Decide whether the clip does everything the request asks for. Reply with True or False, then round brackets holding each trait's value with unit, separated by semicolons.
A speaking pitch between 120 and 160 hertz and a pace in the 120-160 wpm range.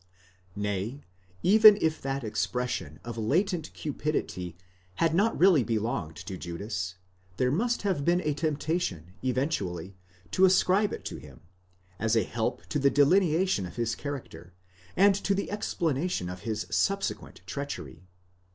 True (140 Hz; 140 wpm)